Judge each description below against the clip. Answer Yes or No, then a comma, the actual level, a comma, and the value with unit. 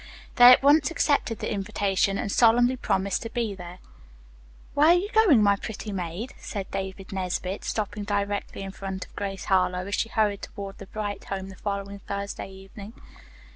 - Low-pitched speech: No, high, 200 Hz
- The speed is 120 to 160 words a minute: No, average, 175 wpm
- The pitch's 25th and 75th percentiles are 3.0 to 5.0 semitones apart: No, narrow, 2.6 semitones